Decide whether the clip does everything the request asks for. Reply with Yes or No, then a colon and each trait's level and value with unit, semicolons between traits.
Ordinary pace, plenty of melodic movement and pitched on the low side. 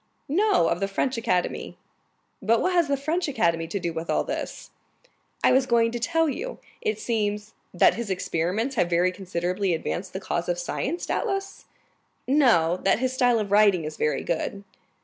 No: average, 180 wpm; wide, 7.2 semitones; high, 210 Hz